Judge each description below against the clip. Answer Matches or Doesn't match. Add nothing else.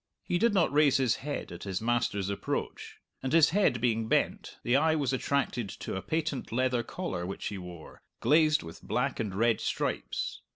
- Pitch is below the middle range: Matches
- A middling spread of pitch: Doesn't match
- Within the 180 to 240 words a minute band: Matches